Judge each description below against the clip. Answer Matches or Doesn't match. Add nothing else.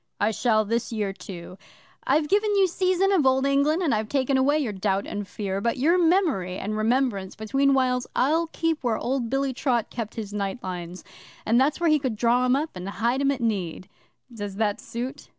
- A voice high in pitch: Matches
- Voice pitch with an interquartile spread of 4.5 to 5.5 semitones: Matches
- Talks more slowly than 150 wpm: Doesn't match